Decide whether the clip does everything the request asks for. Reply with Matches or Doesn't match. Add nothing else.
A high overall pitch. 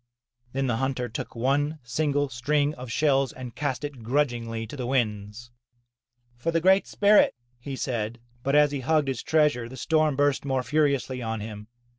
Doesn't match